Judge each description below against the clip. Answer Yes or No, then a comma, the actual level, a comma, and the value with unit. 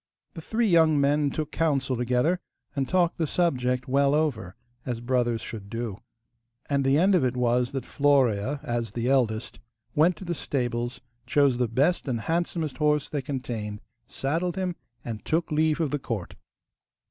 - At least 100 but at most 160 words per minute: No, average, 170 wpm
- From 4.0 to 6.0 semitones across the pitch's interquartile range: Yes, average, 4.4 semitones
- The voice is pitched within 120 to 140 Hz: Yes, low, 135 Hz